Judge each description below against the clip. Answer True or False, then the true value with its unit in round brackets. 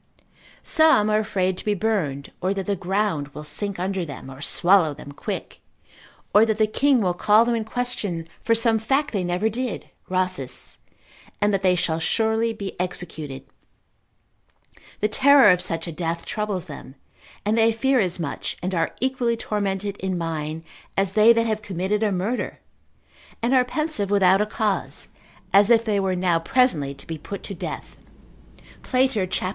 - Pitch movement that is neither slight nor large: True (3.9 semitones)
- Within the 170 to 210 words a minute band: True (175 wpm)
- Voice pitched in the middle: False (200 Hz)